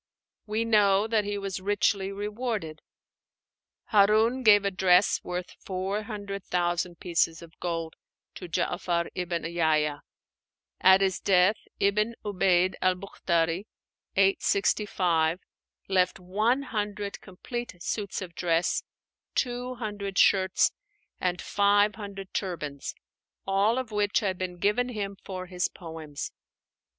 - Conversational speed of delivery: No, slow, 120 wpm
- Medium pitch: No, high, 195 Hz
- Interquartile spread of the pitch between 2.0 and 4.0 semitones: Yes, average, 2.7 semitones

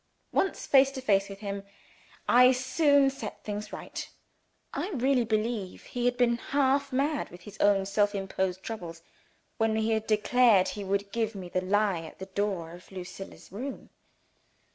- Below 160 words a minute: No, average, 165 wpm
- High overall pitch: Yes, high, 215 Hz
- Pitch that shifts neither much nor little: Yes, average, 4.4 semitones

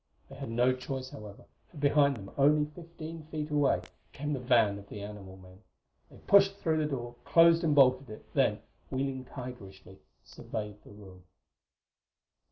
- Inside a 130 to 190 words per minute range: Yes, average, 160 wpm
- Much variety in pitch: Yes, wide, 6.1 semitones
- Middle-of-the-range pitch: No, low, 130 Hz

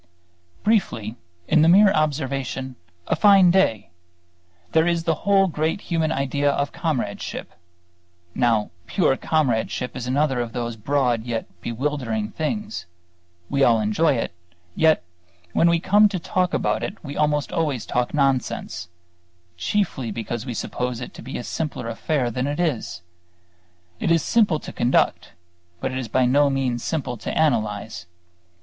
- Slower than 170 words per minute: Yes, average, 155 wpm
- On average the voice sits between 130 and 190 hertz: Yes, medium, 140 Hz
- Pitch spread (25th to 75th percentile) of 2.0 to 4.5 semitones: No, average, 5.2 semitones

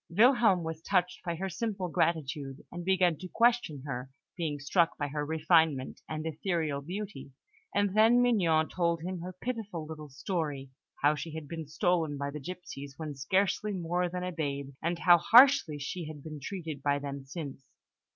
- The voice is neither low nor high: Yes, medium, 165 Hz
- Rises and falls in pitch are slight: No, average, 3.8 semitones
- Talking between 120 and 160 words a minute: No, average, 175 wpm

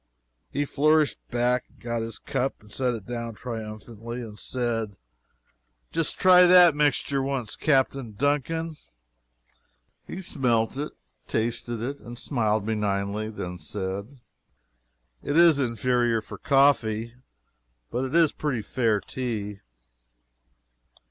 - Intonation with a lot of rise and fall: No, average, 4.2 semitones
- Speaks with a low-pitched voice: Yes, low, 120 Hz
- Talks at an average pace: No, slow, 115 wpm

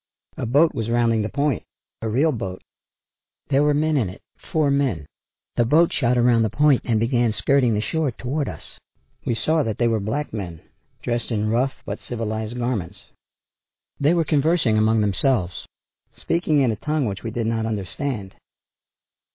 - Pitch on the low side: Yes, low, 120 Hz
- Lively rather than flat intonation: No, average, 4.6 semitones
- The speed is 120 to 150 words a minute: No, average, 175 wpm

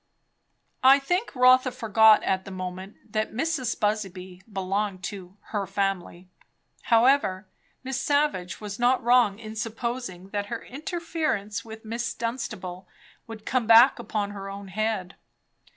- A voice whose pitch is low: No, high, 215 Hz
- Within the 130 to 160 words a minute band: Yes, slow, 135 wpm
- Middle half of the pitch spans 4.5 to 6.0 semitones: No, average, 4.1 semitones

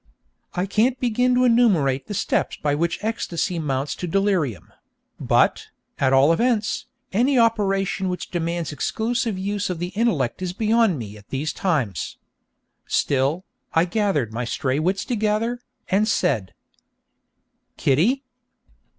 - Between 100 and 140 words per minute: Yes, slow, 135 wpm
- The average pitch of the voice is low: No, medium, 185 Hz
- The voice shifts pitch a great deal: Yes, wide, 7.0 semitones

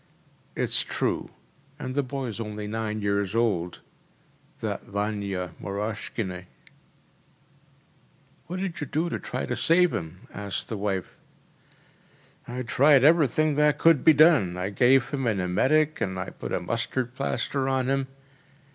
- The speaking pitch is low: Yes, low, 115 Hz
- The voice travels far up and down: Yes, wide, 5.8 semitones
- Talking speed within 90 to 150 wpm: Yes, average, 140 wpm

